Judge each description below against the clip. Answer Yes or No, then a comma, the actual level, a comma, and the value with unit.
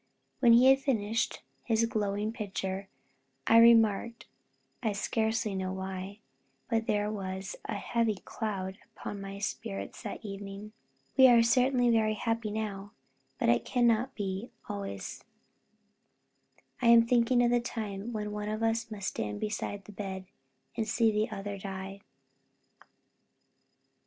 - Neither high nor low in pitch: No, high, 215 Hz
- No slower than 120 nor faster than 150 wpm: Yes, average, 140 wpm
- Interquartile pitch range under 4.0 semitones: Yes, average, 2.8 semitones